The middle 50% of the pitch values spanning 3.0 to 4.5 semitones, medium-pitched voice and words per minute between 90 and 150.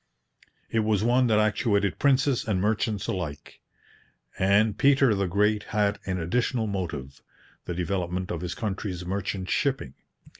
No: average, 3.3 semitones; low, 100 Hz; average, 140 wpm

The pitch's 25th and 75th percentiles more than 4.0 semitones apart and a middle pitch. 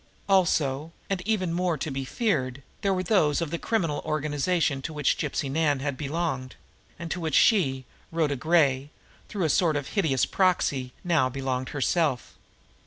Yes: average, 4.4 semitones; medium, 155 Hz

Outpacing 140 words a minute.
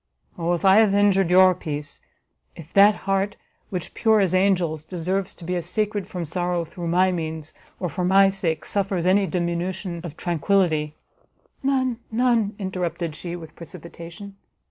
Yes: average, 165 wpm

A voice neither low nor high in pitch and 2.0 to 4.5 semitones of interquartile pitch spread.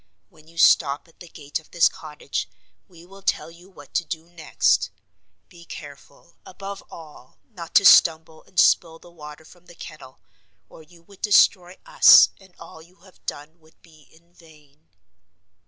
Yes: medium, 165 Hz; narrow, 2.4 semitones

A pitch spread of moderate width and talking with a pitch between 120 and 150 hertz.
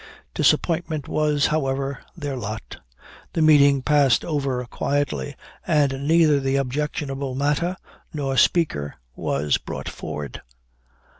No: narrow, 2.1 semitones; medium, 140 Hz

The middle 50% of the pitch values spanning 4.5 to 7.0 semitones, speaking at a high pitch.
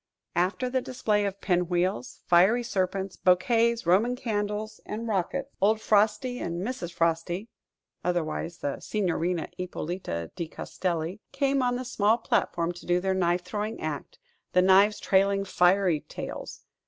No: average, 3.9 semitones; high, 195 Hz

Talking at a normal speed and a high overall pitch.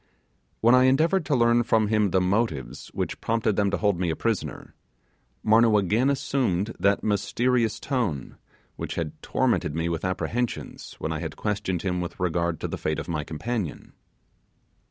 No: average, 170 wpm; low, 105 Hz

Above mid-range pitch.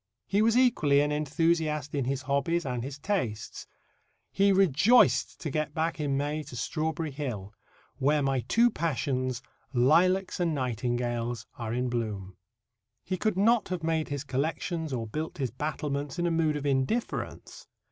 No: medium, 145 Hz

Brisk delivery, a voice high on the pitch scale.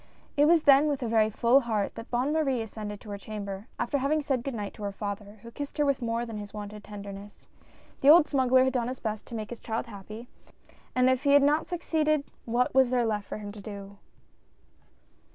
Yes: fast, 225 wpm; high, 235 Hz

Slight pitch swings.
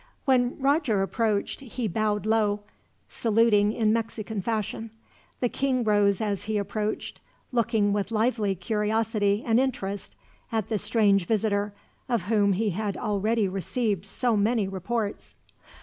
Yes: narrow, 2.0 semitones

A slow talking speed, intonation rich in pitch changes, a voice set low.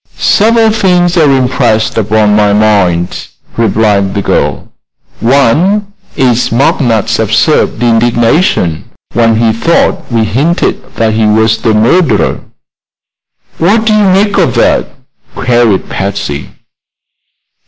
Yes: slow, 110 wpm; wide, 7.7 semitones; low, 115 Hz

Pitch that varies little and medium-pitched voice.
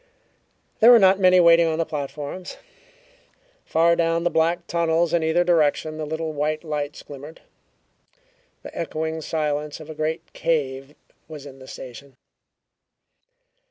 Yes: narrow, 2.2 semitones; medium, 160 Hz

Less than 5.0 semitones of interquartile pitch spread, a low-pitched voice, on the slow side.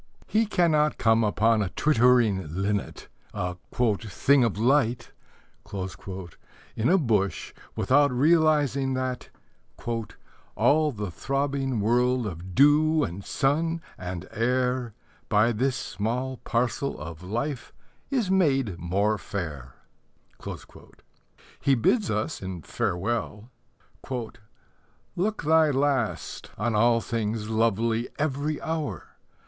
No: average, 5.3 semitones; low, 120 Hz; slow, 105 wpm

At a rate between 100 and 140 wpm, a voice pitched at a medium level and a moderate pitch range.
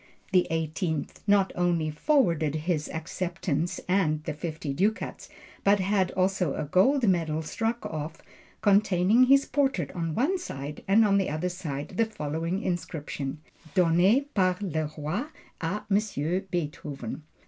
Yes: slow, 135 wpm; medium, 175 Hz; average, 4.4 semitones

